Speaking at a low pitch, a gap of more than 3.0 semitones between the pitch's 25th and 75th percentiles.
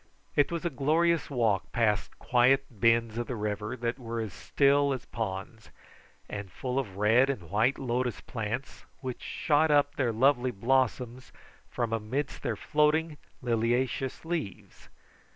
Yes: low, 125 Hz; average, 3.6 semitones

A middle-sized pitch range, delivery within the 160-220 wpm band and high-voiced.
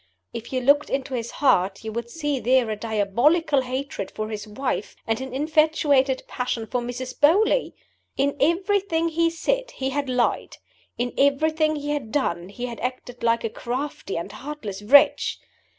Yes: average, 4.2 semitones; average, 170 wpm; very high, 260 Hz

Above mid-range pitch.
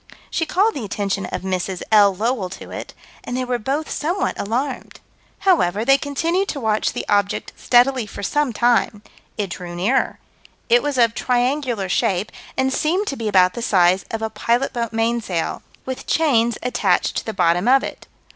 Yes: high, 235 Hz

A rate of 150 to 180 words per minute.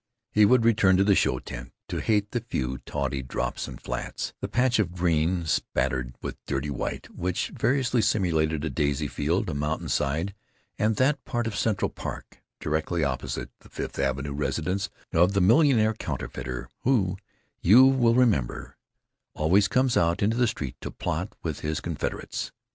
Yes: average, 160 wpm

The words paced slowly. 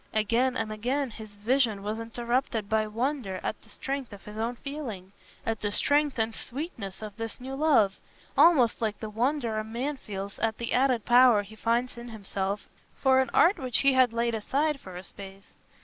No: average, 190 wpm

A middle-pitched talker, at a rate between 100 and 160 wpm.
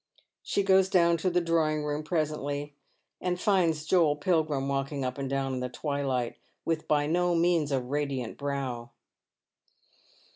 Yes: medium, 150 Hz; average, 150 wpm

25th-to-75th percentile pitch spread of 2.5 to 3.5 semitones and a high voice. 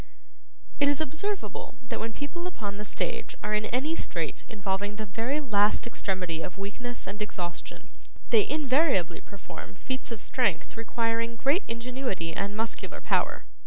No: average, 4.6 semitones; high, 225 Hz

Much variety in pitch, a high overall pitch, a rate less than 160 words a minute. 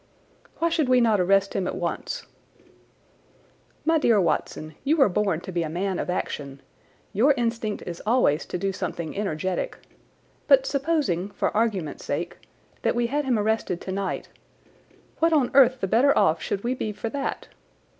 No: wide, 6.1 semitones; high, 210 Hz; average, 165 wpm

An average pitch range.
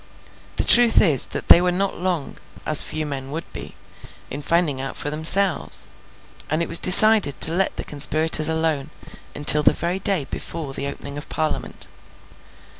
Yes: average, 3.6 semitones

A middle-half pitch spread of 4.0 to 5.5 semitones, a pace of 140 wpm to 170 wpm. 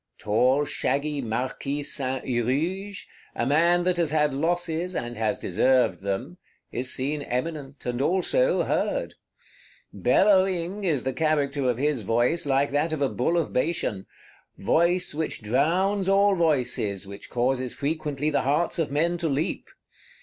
Yes: average, 5.0 semitones; average, 145 wpm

